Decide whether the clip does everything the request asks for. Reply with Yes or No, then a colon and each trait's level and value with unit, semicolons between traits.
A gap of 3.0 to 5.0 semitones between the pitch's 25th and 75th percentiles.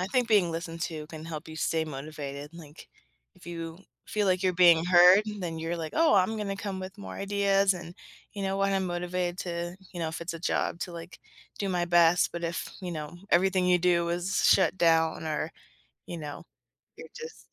No: narrow, 2.5 semitones